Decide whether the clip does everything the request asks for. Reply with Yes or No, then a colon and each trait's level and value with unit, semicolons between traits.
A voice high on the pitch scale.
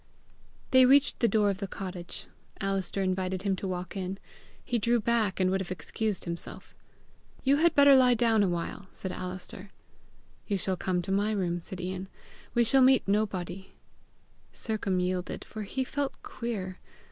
Yes: high, 195 Hz